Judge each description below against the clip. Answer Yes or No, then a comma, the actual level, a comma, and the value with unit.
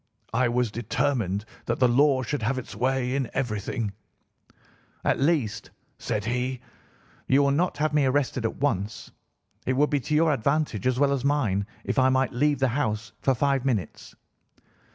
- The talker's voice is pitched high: No, low, 130 Hz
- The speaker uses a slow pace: No, average, 175 wpm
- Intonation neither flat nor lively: Yes, average, 3.4 semitones